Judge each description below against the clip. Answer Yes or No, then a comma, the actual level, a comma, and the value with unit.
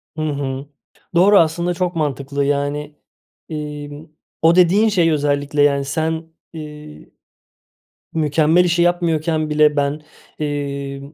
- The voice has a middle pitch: Yes, medium, 150 Hz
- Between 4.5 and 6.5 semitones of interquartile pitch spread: No, narrow, 2.4 semitones